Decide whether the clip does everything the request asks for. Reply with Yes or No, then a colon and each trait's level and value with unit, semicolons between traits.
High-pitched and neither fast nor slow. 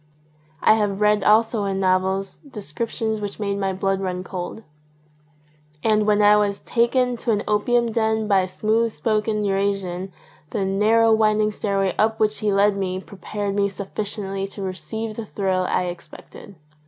Yes: high, 205 Hz; average, 165 wpm